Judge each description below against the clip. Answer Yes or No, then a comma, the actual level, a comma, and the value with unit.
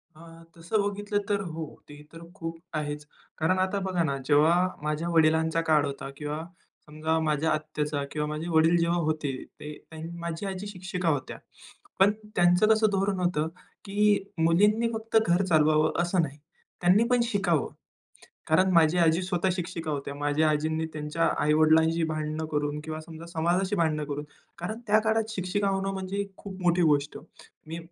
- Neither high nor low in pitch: Yes, medium, 165 Hz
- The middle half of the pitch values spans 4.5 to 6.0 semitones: No, average, 3.4 semitones